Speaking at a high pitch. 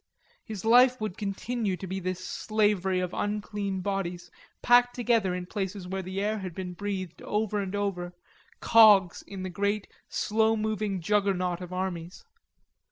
Yes: high, 195 Hz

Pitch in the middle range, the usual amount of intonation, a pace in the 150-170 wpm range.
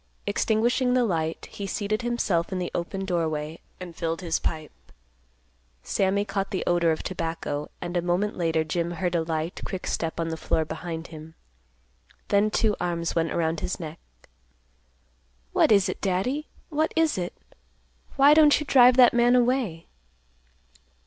Yes: medium, 180 Hz; average, 4.8 semitones; average, 160 wpm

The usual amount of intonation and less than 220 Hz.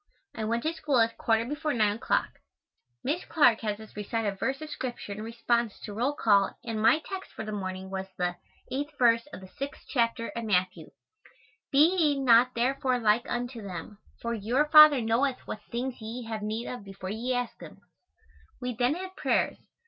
No: average, 3.7 semitones; high, 235 Hz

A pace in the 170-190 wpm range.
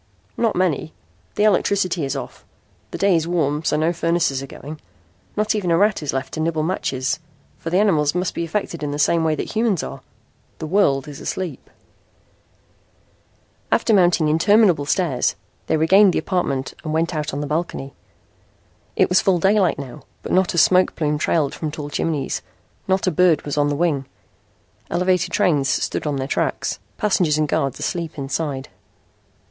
Yes: average, 175 wpm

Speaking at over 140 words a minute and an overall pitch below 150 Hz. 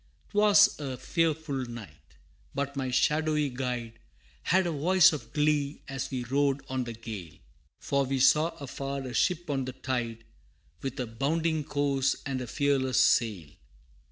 Yes: average, 155 wpm; low, 135 Hz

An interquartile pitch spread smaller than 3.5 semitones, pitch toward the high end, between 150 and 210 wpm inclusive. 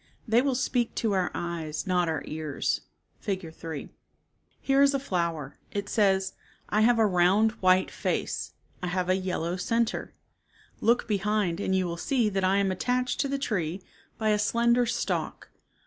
No: average, 4.6 semitones; high, 195 Hz; average, 175 wpm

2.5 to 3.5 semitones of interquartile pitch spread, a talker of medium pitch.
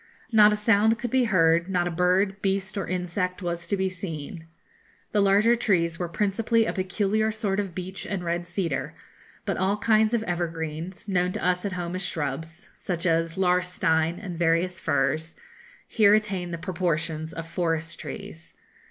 Yes: average, 3.1 semitones; medium, 180 Hz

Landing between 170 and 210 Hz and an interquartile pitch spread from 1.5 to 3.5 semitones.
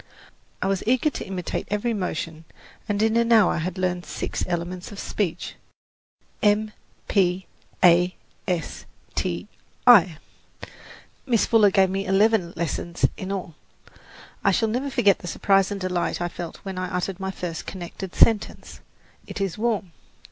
Yes: high, 190 Hz; average, 2.8 semitones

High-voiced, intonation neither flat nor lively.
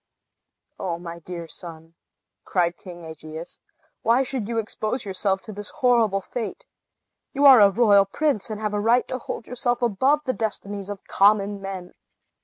Yes: high, 205 Hz; average, 4.3 semitones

